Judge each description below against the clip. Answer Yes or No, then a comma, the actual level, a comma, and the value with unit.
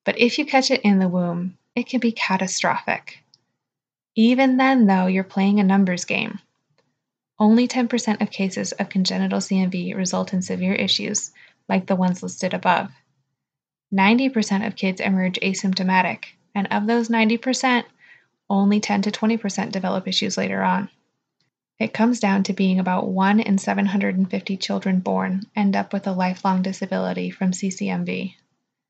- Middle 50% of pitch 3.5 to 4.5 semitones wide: No, narrow, 2.5 semitones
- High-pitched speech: Yes, high, 195 Hz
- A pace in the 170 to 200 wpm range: No, average, 150 wpm